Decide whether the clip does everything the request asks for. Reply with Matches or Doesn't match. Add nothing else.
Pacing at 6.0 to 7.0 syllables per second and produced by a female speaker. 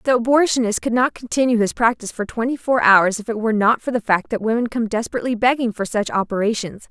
Matches